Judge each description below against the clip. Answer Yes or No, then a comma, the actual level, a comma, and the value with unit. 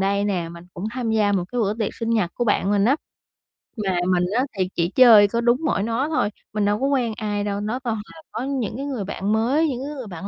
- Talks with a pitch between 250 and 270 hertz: No, high, 215 Hz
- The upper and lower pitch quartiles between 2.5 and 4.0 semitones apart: Yes, average, 3.7 semitones